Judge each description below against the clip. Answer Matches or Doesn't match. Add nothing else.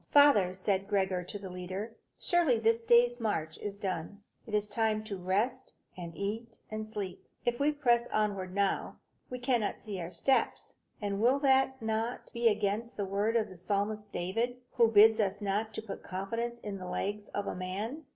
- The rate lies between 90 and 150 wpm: Doesn't match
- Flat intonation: Doesn't match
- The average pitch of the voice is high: Matches